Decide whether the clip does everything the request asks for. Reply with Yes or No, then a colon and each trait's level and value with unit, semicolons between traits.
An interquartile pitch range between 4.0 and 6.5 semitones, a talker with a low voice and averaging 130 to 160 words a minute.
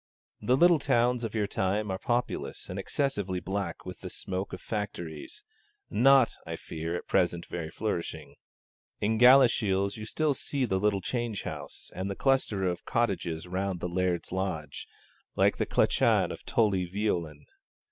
Yes: average, 4.7 semitones; low, 100 Hz; average, 155 wpm